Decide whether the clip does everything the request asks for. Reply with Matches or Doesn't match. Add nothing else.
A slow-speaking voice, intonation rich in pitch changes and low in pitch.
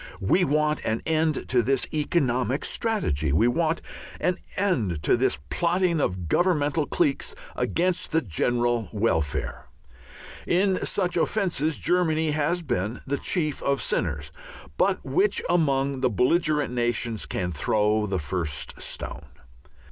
Doesn't match